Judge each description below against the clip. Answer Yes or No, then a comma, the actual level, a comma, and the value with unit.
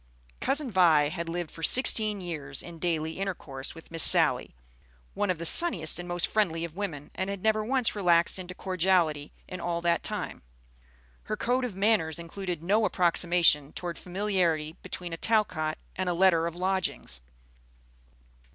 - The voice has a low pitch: No, medium, 175 Hz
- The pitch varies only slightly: No, average, 3.1 semitones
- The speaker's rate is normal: Yes, average, 160 wpm